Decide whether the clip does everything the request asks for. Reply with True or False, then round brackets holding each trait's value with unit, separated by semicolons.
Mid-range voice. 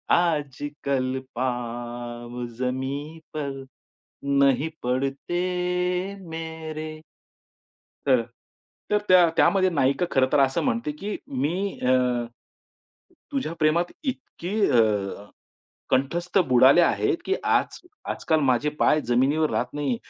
True (145 Hz)